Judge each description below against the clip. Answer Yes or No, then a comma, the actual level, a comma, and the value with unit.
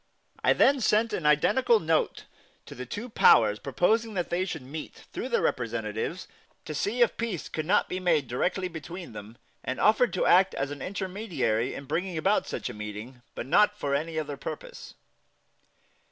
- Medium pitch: Yes, medium, 165 Hz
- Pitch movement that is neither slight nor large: No, wide, 7.3 semitones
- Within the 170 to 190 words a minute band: Yes, average, 180 wpm